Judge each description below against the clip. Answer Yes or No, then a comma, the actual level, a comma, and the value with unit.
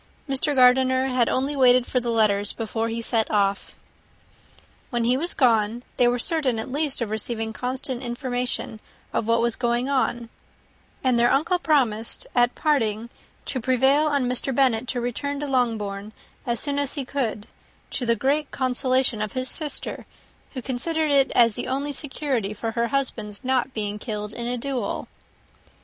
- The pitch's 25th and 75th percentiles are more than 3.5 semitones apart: No, average, 2.9 semitones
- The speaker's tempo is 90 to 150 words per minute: No, average, 170 wpm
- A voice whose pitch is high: Yes, high, 245 Hz